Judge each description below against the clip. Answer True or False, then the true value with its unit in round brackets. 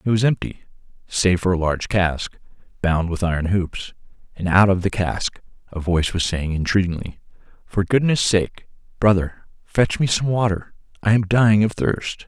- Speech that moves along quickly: False (170 wpm)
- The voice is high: False (95 Hz)